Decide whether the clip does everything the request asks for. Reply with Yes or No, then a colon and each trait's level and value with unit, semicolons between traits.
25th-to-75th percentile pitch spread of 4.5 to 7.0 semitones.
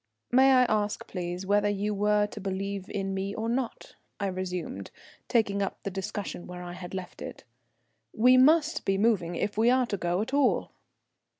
No: average, 3.3 semitones